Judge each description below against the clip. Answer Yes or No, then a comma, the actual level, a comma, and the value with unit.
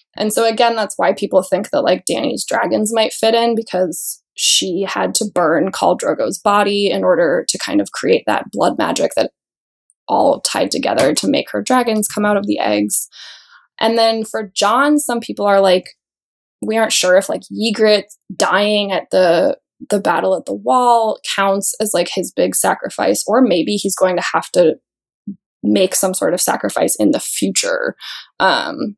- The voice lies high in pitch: Yes, high, 215 Hz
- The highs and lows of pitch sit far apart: No, average, 3.2 semitones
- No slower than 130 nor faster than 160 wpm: No, average, 180 wpm